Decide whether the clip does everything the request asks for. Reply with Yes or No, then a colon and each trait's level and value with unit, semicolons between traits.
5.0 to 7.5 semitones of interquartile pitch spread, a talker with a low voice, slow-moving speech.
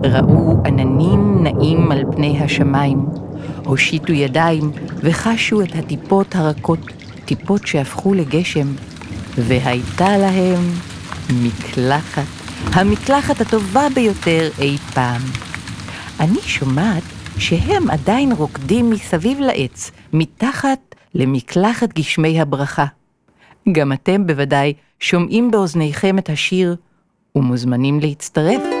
No: wide, 5.6 semitones; medium, 155 Hz; slow, 90 wpm